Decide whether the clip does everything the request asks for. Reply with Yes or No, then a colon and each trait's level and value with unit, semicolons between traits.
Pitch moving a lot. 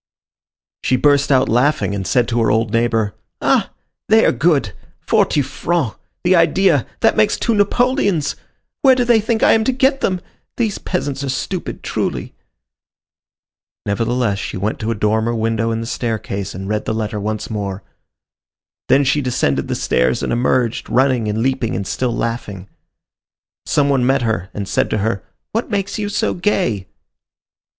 Yes: wide, 8.0 semitones